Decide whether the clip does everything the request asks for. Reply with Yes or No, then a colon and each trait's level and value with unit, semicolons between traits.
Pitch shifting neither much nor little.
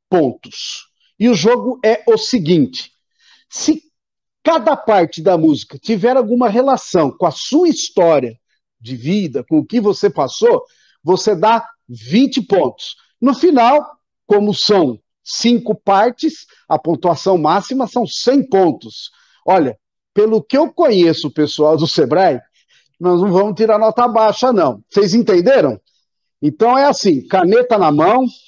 No: wide, 5.7 semitones